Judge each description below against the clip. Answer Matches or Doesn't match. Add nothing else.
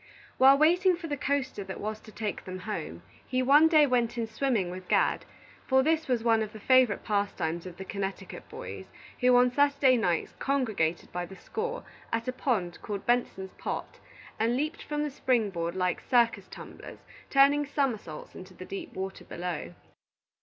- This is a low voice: Doesn't match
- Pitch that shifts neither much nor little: Doesn't match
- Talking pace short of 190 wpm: Matches